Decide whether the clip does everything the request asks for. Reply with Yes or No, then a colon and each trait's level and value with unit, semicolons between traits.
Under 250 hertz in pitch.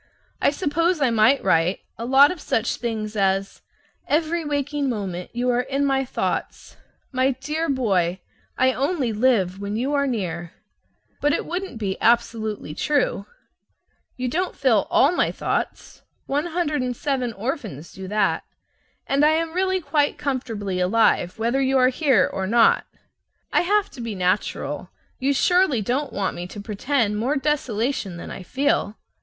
No: very high, 255 Hz